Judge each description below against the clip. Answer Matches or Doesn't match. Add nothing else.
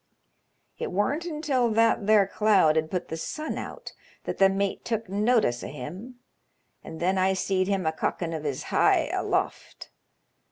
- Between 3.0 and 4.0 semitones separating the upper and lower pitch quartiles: Doesn't match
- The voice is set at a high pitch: Matches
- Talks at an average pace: Matches